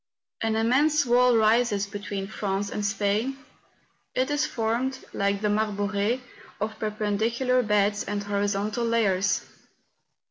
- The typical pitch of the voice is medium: No, high, 215 Hz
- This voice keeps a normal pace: No, slow, 115 wpm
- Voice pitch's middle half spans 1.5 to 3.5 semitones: Yes, average, 2.8 semitones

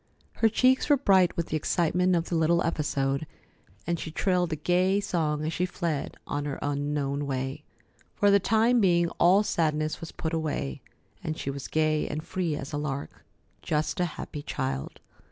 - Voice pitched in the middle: Yes, medium, 160 Hz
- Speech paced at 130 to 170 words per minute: No, average, 180 wpm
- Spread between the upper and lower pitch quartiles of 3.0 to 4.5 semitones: Yes, average, 3.5 semitones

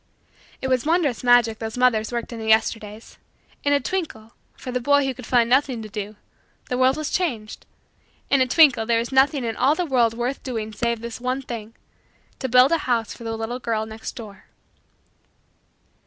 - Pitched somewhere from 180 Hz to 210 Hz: No, high, 240 Hz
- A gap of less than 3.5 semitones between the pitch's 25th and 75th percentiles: Yes, average, 2.8 semitones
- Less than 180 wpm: No, average, 195 wpm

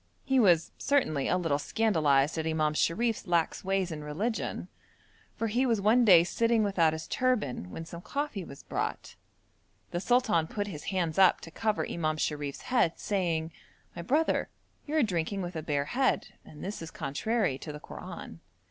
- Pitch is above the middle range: No, medium, 175 Hz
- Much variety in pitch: Yes, wide, 5.9 semitones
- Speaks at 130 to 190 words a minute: Yes, average, 175 wpm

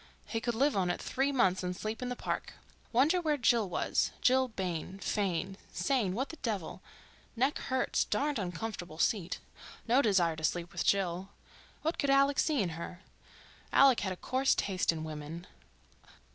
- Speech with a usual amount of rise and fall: No, wide, 6.6 semitones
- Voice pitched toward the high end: Yes, high, 210 Hz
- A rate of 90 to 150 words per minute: No, average, 160 wpm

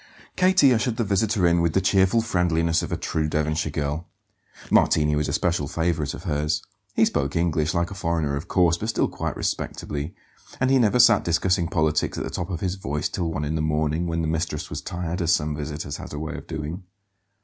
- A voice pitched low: Yes, very low, 85 Hz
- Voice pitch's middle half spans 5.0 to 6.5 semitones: No, average, 3.2 semitones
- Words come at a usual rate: No, fast, 215 wpm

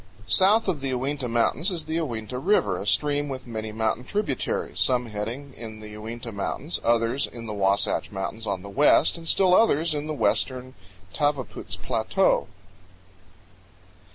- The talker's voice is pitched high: No, low, 125 Hz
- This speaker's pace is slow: No, average, 155 wpm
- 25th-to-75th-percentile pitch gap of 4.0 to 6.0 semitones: Yes, average, 5.1 semitones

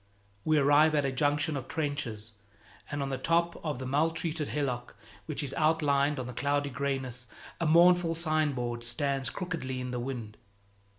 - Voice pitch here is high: No, medium, 145 Hz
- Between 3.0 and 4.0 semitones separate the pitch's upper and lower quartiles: Yes, average, 3.3 semitones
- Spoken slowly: No, average, 165 wpm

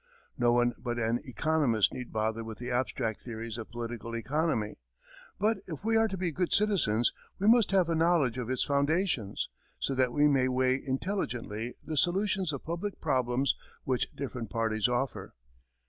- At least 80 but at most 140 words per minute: No, average, 170 wpm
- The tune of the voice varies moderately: No, wide, 6.0 semitones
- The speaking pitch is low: Yes, low, 130 Hz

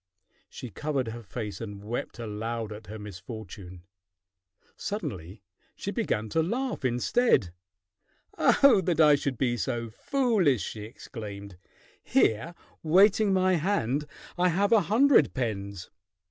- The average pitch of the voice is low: Yes, low, 120 Hz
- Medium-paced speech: No, slow, 125 wpm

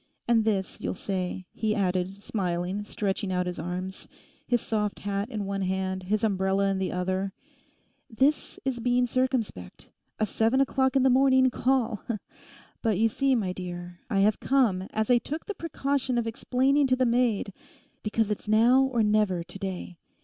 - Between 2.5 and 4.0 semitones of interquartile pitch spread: No, average, 4.9 semitones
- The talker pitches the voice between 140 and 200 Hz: No, high, 215 Hz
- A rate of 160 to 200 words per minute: Yes, average, 165 wpm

